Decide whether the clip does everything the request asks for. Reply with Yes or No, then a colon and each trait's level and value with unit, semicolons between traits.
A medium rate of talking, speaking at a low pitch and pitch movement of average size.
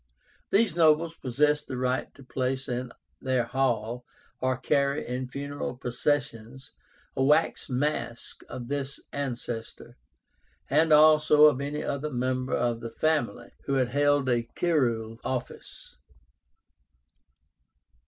No: slow, 120 wpm; low, 130 Hz; average, 3.1 semitones